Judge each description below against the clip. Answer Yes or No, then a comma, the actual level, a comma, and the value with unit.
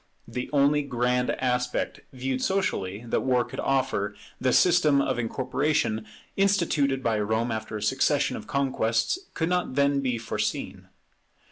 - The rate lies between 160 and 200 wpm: No, average, 140 wpm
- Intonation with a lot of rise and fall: No, average, 3.4 semitones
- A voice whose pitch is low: Yes, low, 130 Hz